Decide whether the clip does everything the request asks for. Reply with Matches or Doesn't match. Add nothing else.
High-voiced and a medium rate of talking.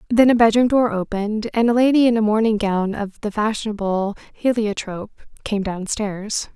Matches